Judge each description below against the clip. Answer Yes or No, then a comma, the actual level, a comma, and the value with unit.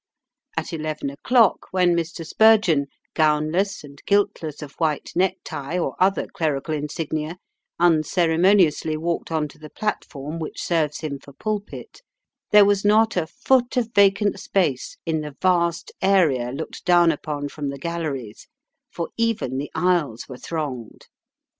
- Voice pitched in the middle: Yes, medium, 165 Hz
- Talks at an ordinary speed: Yes, average, 145 wpm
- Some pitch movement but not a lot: Yes, average, 4.1 semitones